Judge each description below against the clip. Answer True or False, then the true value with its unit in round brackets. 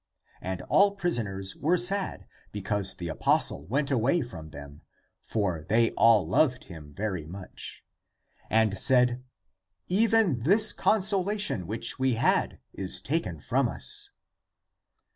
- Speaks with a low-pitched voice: True (110 Hz)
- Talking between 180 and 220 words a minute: False (135 wpm)